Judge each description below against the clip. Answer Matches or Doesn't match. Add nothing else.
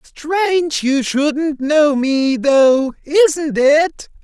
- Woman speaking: Doesn't match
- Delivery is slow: Matches